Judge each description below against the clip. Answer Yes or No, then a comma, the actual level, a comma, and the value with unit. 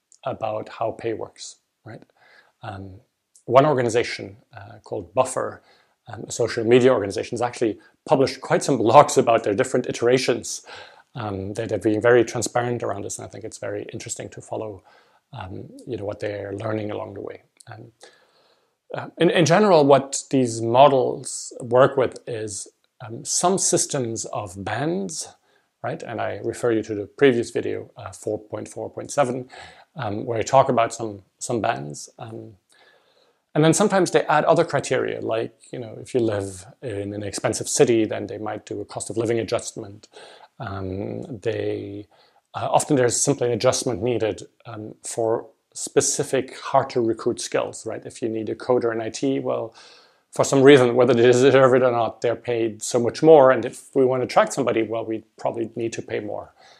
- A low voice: Yes, low, 115 Hz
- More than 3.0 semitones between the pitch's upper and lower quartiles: Yes, average, 3.4 semitones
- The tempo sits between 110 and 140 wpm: No, average, 175 wpm